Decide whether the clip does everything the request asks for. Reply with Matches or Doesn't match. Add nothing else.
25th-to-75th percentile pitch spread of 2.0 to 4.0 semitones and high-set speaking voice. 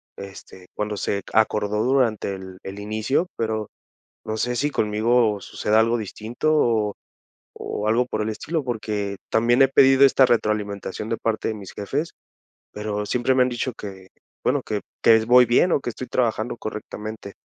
Doesn't match